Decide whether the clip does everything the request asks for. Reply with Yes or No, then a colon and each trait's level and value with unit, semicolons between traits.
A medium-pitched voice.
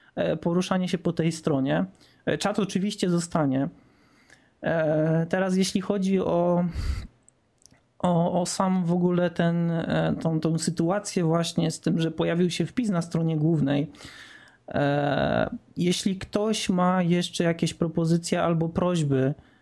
Yes: medium, 175 Hz